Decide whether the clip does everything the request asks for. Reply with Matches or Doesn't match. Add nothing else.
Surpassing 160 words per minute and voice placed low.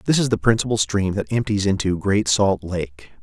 Matches